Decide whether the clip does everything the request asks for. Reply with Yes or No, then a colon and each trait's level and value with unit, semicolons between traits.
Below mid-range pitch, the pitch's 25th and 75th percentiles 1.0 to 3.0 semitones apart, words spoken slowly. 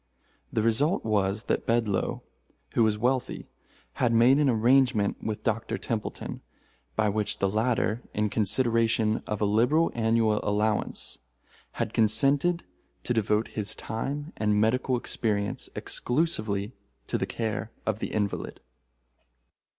Yes: low, 110 Hz; narrow, 2.5 semitones; slow, 125 wpm